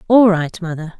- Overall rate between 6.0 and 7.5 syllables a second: No, 5.0 syllables/s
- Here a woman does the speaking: Yes, female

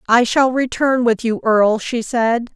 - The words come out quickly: No, average, 190 wpm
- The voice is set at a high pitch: Yes, high, 235 Hz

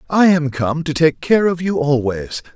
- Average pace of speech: No, fast, 210 wpm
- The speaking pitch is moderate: Yes, medium, 155 Hz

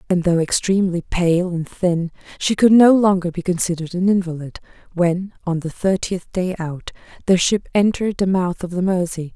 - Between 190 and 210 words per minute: No, average, 180 wpm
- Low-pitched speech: No, medium, 180 Hz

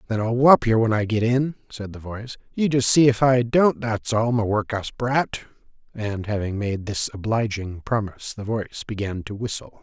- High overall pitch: No, low, 115 Hz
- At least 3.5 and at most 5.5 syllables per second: Yes, 5.1 syllables/s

